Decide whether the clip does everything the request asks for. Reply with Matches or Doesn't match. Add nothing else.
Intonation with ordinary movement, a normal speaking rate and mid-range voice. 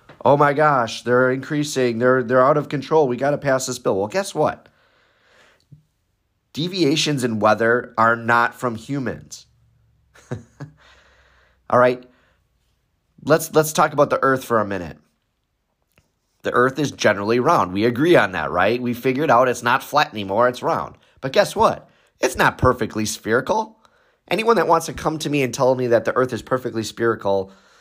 Doesn't match